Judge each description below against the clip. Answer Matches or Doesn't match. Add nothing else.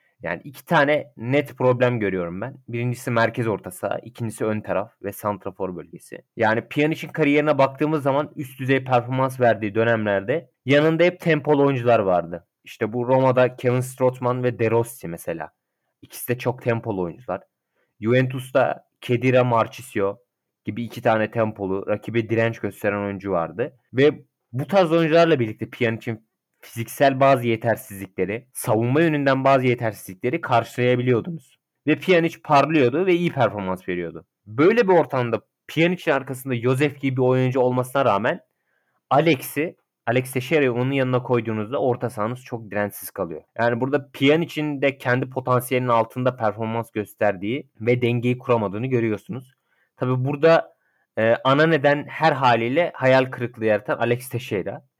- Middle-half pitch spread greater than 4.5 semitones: Doesn't match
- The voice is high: Doesn't match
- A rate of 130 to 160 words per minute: Matches